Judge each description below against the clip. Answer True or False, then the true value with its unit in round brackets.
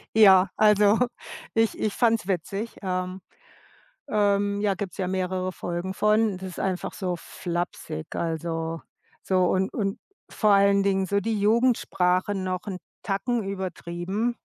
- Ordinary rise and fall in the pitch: False (2.3 semitones)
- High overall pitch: True (195 Hz)